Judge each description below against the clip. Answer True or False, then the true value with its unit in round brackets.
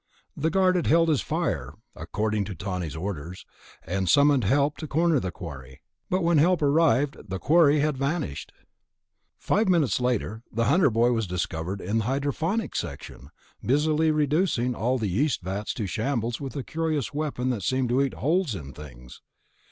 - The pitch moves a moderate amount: False (7.6 semitones)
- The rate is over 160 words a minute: True (170 wpm)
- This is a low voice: True (130 Hz)